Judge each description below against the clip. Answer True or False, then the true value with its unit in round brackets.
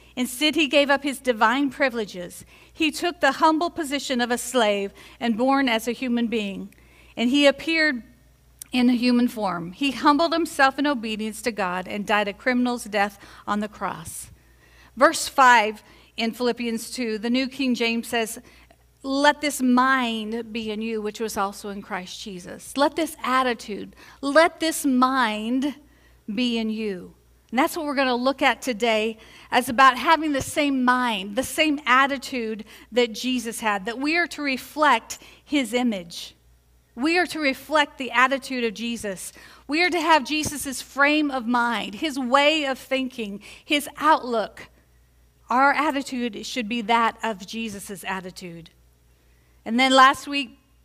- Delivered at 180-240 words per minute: False (160 wpm)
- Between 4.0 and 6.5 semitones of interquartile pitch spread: True (4.3 semitones)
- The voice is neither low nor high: False (245 Hz)